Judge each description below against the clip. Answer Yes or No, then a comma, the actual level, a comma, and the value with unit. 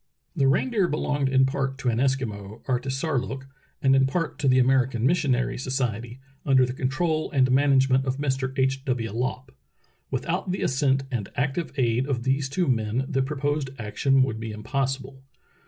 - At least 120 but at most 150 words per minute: No, average, 170 wpm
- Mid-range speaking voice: No, low, 130 Hz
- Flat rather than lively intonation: Yes, narrow, 1.5 semitones